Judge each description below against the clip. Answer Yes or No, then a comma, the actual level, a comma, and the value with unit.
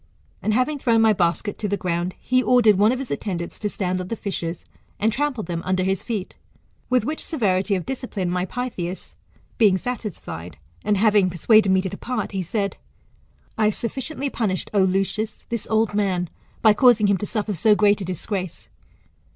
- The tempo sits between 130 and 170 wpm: No, average, 185 wpm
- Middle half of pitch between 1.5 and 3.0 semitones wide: No, average, 3.6 semitones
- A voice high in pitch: Yes, high, 205 Hz